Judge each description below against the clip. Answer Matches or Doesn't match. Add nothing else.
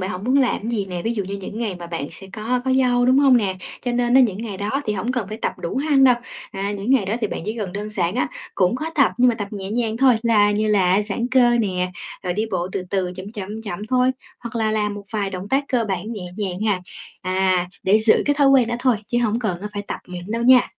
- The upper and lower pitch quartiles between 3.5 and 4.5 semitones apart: Matches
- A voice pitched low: Doesn't match